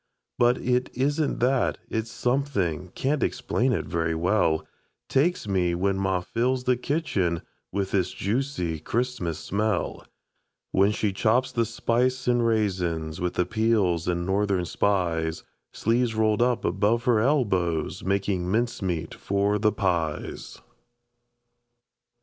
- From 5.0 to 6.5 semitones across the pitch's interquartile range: Yes, wide, 5.4 semitones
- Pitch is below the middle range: Yes, low, 105 Hz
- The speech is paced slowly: Yes, slow, 125 wpm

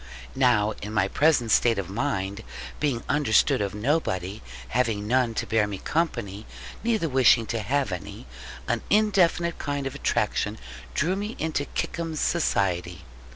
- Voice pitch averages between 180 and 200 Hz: No, low, 120 Hz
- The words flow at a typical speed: Yes, average, 145 wpm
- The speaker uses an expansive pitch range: Yes, wide, 6.9 semitones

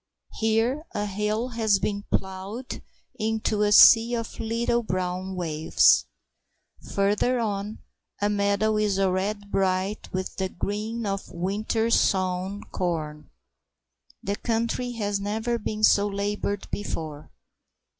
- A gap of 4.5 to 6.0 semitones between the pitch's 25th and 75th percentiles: No, narrow, 2.6 semitones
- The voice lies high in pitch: Yes, high, 205 Hz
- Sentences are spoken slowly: Yes, slow, 115 wpm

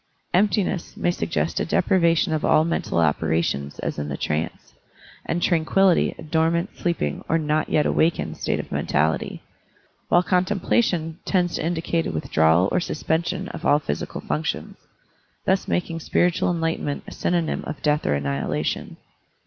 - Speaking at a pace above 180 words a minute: No, average, 150 wpm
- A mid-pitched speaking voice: Yes, medium, 160 Hz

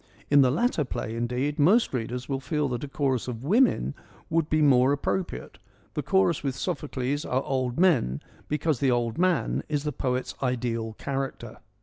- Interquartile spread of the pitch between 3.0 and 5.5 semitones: Yes, average, 3.4 semitones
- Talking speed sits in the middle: Yes, average, 170 wpm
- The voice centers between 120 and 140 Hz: Yes, low, 135 Hz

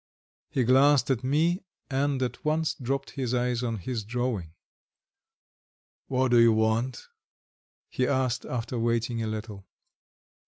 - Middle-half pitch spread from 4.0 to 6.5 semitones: No, narrow, 2.5 semitones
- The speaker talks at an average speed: No, slow, 130 wpm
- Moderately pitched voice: No, low, 125 Hz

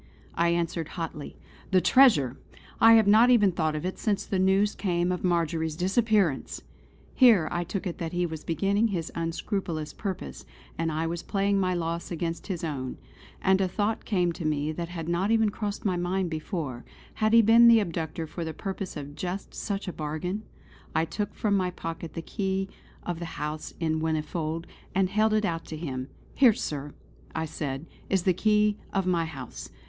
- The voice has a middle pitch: Yes, medium, 175 Hz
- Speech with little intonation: No, average, 3.6 semitones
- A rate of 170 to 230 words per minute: Yes, average, 185 wpm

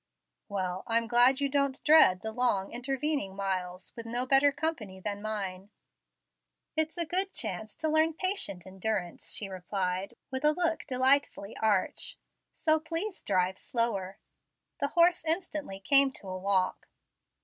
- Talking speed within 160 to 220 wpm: No, average, 145 wpm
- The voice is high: Yes, high, 235 Hz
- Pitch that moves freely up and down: Yes, wide, 7.8 semitones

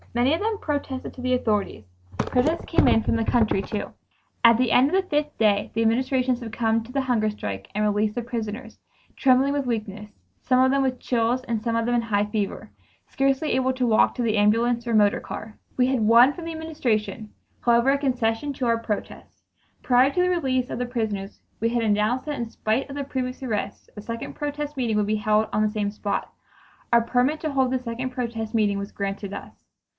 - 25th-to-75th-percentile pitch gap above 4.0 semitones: No, average, 3.3 semitones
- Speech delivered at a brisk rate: Yes, fast, 220 wpm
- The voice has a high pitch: Yes, high, 235 Hz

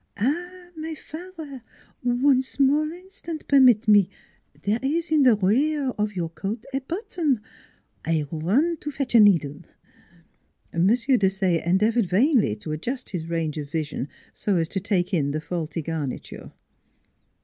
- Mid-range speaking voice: No, high, 215 Hz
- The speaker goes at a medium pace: Yes, average, 150 wpm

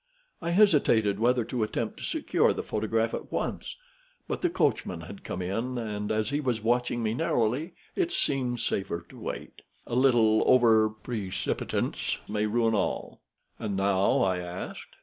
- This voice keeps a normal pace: Yes, average, 160 wpm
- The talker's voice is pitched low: Yes, low, 110 Hz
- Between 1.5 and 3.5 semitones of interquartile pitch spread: Yes, average, 3.2 semitones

